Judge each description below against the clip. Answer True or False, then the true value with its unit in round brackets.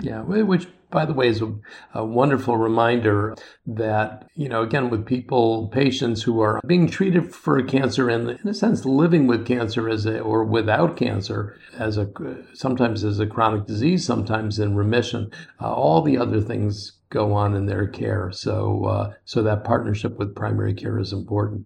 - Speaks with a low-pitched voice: True (115 Hz)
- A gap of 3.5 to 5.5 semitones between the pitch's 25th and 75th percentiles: False (2.9 semitones)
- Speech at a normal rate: True (175 wpm)